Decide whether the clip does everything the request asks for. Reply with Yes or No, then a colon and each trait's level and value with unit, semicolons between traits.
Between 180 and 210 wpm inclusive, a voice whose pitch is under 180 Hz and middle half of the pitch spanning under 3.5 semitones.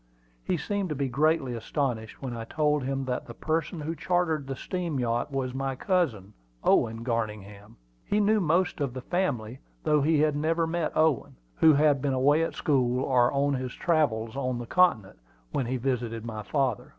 No: average, 185 wpm; low, 135 Hz; average, 4.6 semitones